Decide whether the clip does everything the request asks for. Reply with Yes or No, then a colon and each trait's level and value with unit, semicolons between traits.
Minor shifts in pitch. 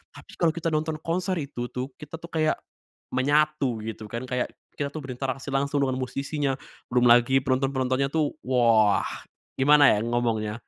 No: average, 3.5 semitones